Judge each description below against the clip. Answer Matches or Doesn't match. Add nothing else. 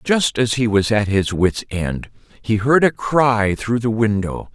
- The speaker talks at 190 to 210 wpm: Matches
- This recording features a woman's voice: Doesn't match